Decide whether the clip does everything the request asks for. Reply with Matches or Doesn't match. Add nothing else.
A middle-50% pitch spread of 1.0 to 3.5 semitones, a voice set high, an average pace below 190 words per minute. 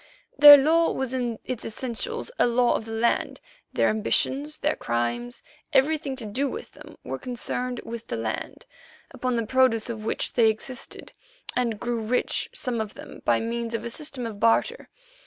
Matches